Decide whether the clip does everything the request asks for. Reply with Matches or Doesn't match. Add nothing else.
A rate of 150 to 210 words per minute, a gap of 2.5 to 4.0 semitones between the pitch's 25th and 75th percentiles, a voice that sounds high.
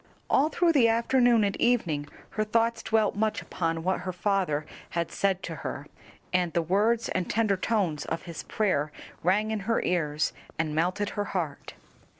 Doesn't match